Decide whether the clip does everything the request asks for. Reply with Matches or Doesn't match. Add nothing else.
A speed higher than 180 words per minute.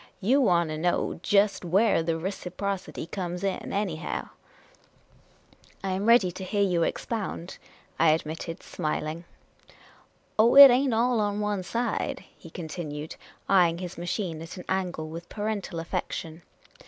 Doesn't match